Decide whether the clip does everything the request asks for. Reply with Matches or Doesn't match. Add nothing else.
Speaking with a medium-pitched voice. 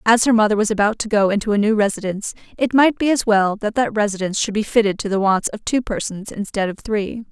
Doesn't match